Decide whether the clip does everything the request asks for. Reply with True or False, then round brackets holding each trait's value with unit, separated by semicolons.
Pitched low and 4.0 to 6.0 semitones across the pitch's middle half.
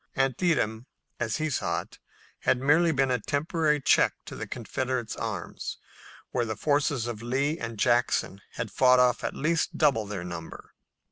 True (130 Hz; 4.3 semitones)